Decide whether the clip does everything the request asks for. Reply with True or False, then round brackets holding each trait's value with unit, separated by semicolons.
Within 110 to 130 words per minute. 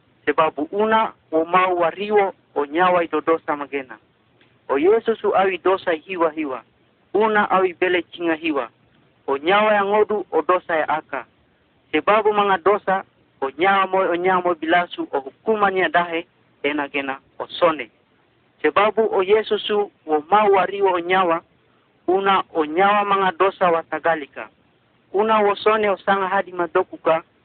True (125 wpm)